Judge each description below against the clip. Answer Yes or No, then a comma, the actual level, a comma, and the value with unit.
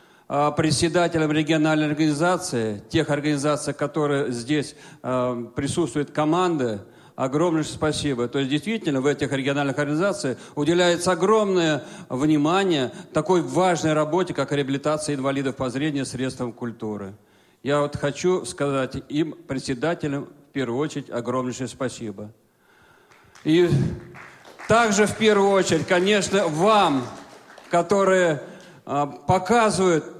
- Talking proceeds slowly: Yes, slow, 105 wpm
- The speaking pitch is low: No, medium, 150 Hz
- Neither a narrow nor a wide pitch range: Yes, average, 4.2 semitones